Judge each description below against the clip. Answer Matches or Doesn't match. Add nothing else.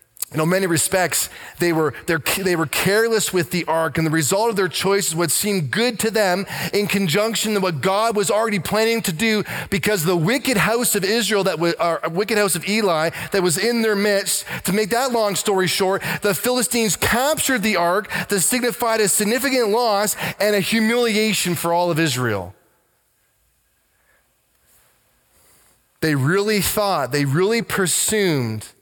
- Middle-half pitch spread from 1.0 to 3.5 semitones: Doesn't match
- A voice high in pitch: Matches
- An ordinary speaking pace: Matches